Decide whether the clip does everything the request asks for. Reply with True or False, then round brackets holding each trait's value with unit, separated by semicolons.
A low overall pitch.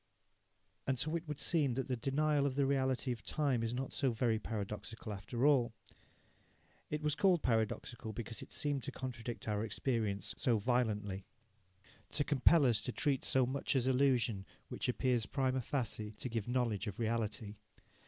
True (125 Hz)